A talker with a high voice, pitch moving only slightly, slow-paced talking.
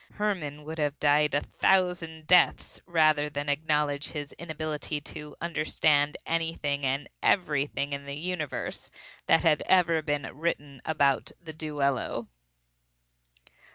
No: medium, 150 Hz; narrow, 2.1 semitones; slow, 120 wpm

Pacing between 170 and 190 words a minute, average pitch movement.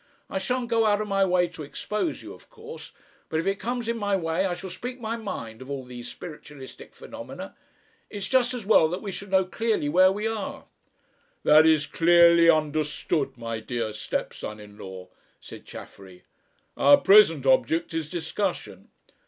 No: average, 175 wpm; wide, 6.6 semitones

